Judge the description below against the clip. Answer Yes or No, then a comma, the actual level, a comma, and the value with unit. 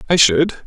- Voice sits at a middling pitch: Yes, medium, 150 Hz